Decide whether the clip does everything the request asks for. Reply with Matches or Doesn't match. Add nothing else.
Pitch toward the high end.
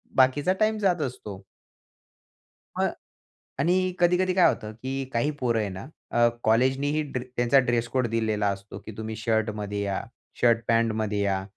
Doesn't match